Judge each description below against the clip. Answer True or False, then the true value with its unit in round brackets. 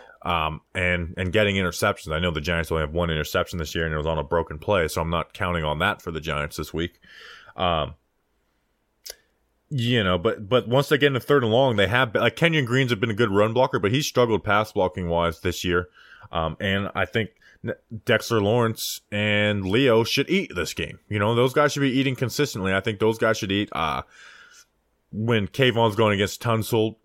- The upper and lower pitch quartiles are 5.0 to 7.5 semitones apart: True (5.3 semitones)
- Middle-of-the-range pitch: False (105 Hz)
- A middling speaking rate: False (215 wpm)